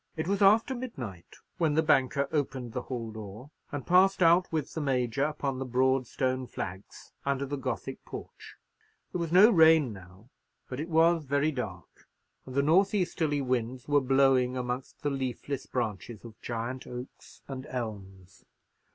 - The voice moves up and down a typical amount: Yes, average, 4.1 semitones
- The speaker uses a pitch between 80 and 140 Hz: Yes, low, 135 Hz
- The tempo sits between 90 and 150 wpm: No, average, 165 wpm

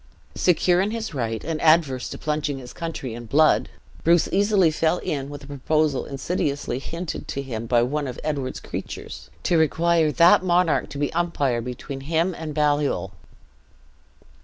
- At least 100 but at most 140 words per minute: No, average, 160 wpm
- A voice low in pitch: No, medium, 150 Hz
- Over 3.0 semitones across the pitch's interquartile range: Yes, average, 3.8 semitones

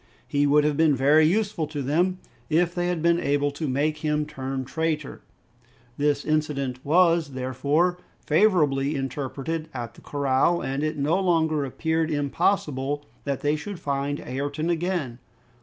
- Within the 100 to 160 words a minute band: Yes, average, 150 wpm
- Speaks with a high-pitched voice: No, medium, 150 Hz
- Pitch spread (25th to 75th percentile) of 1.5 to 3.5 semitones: Yes, average, 2.8 semitones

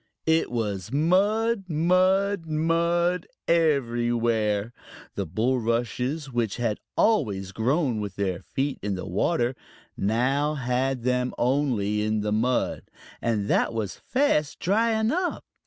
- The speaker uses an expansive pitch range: Yes, wide, 7.1 semitones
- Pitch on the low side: Yes, low, 125 Hz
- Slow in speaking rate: Yes, slow, 115 wpm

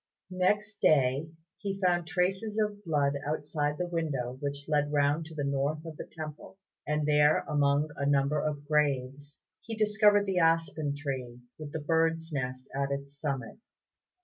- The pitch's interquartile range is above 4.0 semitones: No, average, 2.8 semitones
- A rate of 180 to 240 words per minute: No, average, 160 wpm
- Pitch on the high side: No, medium, 150 Hz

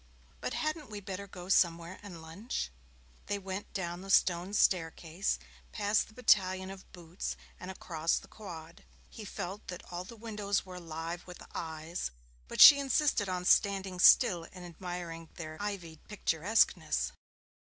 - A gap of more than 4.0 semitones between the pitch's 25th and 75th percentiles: No, average, 3.1 semitones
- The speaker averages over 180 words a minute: No, average, 150 wpm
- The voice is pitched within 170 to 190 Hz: Yes, medium, 185 Hz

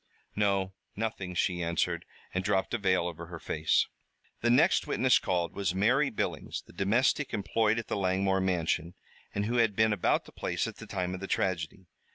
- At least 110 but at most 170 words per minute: No, average, 190 wpm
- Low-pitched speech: Yes, very low, 95 Hz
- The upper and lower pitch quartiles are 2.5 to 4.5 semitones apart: Yes, average, 3.5 semitones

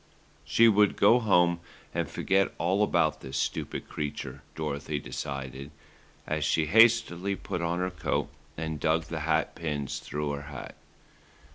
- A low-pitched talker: Yes, very low, 80 Hz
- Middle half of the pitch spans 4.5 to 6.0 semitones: Yes, average, 4.8 semitones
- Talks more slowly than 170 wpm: Yes, average, 145 wpm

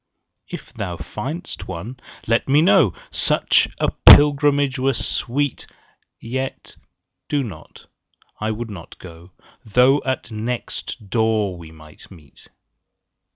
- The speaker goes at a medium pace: No, slow, 120 wpm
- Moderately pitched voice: No, low, 115 Hz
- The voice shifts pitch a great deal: Yes, wide, 6.0 semitones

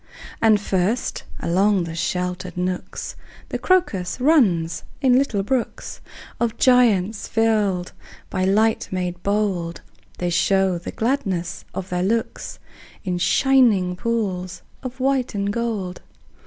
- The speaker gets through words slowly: Yes, slow, 120 wpm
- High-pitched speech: Yes, high, 200 Hz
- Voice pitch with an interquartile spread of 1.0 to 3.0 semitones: No, average, 4.4 semitones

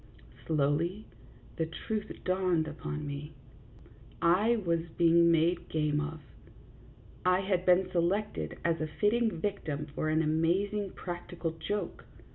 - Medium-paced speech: No, slow, 120 wpm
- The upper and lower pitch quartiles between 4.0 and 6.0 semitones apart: No, average, 3.2 semitones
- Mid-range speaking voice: Yes, medium, 170 Hz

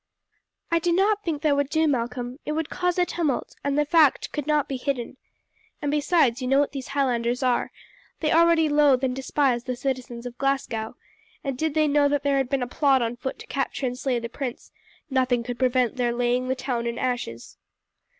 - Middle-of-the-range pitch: No, very high, 270 Hz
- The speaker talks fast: Yes, fast, 210 wpm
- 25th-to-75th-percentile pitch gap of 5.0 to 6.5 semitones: No, average, 3.1 semitones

